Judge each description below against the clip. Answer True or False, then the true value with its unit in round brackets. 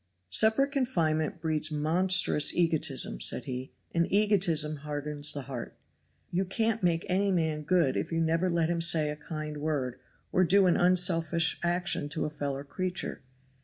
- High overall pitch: False (165 Hz)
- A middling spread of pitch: True (3.3 semitones)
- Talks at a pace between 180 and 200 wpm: False (160 wpm)